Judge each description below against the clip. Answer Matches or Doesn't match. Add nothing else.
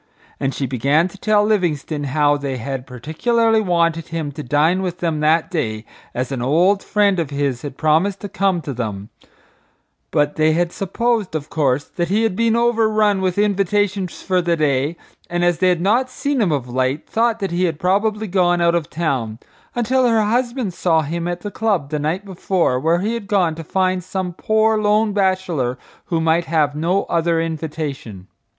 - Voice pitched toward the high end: Doesn't match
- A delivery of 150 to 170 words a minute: Doesn't match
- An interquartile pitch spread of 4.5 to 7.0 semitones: Matches